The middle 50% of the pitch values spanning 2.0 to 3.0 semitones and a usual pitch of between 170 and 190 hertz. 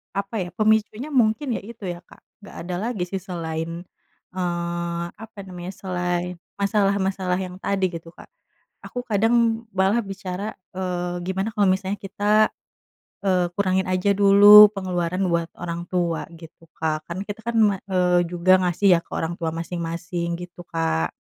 Yes: narrow, 2.6 semitones; medium, 185 Hz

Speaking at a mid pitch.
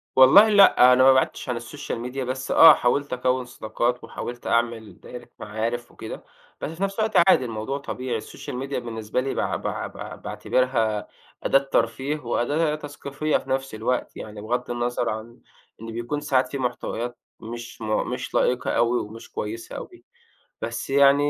No: low, 125 Hz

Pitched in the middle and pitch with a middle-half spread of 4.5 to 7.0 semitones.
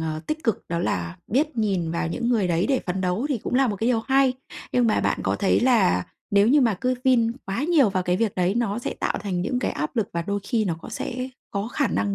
No: high, 215 Hz; wide, 5.4 semitones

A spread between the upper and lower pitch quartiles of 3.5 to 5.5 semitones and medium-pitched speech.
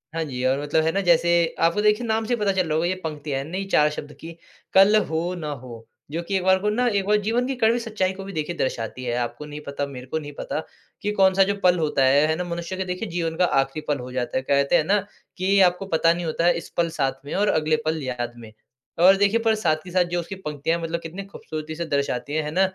Yes: average, 4.6 semitones; medium, 165 Hz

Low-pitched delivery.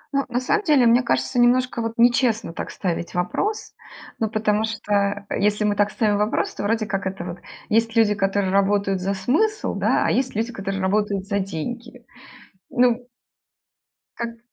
No: high, 215 Hz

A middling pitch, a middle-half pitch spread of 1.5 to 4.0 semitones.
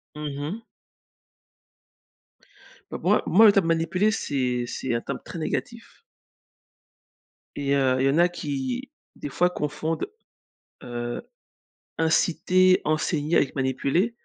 No: medium, 155 Hz; average, 4.9 semitones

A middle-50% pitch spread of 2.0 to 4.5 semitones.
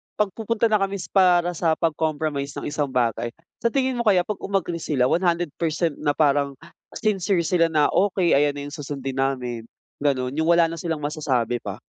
Yes: average, 4.1 semitones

